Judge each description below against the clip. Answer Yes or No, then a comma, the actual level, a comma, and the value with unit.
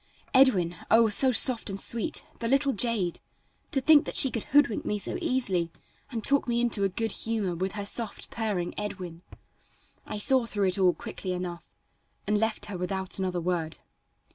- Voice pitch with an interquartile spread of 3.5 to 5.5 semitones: Yes, average, 4.3 semitones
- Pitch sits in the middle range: No, high, 210 Hz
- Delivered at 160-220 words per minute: Yes, average, 180 wpm